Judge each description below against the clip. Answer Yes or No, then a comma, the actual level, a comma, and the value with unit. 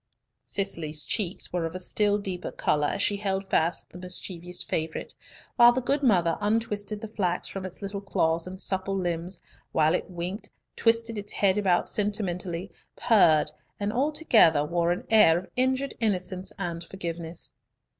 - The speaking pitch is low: No, high, 190 Hz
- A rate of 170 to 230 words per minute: No, average, 160 wpm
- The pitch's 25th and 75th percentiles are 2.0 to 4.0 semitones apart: Yes, average, 3.4 semitones